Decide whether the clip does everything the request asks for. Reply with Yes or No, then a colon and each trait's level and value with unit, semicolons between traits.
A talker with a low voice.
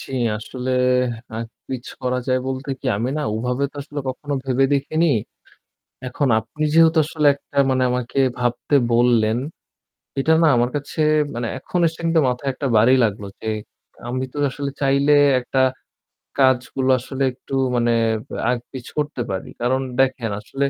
Yes: low, 130 Hz